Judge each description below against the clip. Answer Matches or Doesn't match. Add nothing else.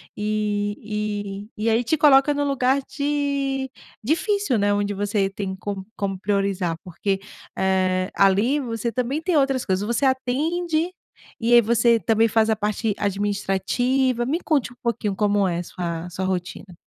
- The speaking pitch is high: Matches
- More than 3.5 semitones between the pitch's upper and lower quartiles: Matches